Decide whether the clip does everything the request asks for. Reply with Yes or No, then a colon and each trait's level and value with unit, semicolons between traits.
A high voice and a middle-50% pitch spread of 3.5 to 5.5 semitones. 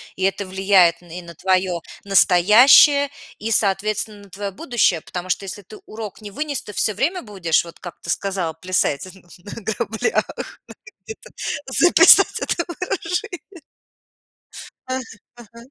Yes: high, 200 Hz; average, 4.5 semitones